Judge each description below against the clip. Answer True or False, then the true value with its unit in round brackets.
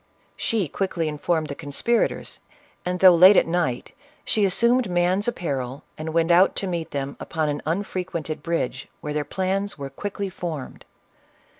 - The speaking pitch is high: False (170 Hz)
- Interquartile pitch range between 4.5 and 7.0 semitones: False (4.1 semitones)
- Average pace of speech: True (155 wpm)